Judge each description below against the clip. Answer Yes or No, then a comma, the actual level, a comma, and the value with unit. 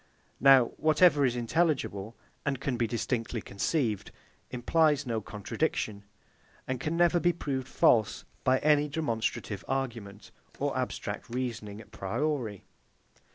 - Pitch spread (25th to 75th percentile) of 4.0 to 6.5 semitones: Yes, average, 4.9 semitones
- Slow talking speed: Yes, slow, 120 wpm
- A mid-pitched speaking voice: No, low, 125 Hz